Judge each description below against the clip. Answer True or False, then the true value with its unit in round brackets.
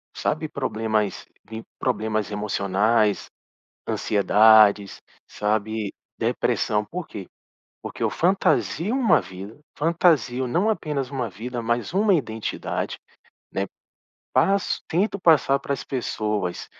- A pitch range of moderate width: False (6.6 semitones)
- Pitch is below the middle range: True (115 Hz)